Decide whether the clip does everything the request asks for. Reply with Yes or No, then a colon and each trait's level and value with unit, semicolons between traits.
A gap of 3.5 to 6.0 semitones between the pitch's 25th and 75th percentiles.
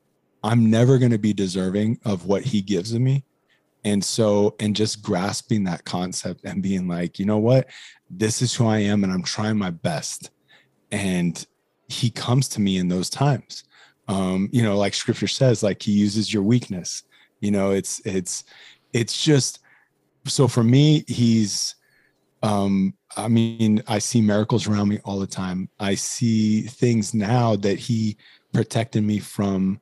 No: average, 2.9 semitones